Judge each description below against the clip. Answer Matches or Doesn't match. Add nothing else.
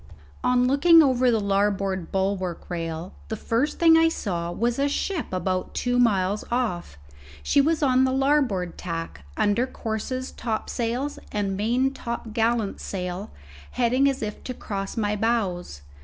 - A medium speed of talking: Matches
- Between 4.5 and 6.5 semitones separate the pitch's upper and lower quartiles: Matches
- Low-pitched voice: Doesn't match